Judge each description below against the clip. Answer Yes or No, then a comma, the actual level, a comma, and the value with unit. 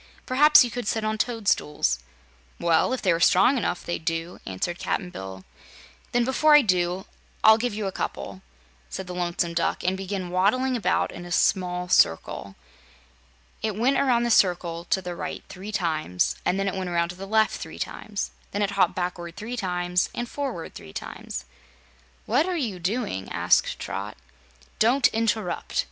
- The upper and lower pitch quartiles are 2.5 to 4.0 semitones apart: No, average, 4.6 semitones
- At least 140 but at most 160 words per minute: No, average, 175 wpm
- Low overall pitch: No, high, 190 Hz